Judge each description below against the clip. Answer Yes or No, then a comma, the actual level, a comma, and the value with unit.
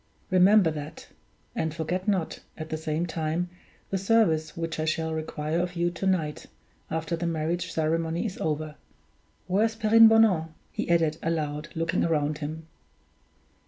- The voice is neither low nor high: Yes, medium, 165 Hz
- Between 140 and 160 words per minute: Yes, average, 155 wpm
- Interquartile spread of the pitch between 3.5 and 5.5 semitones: No, narrow, 2.4 semitones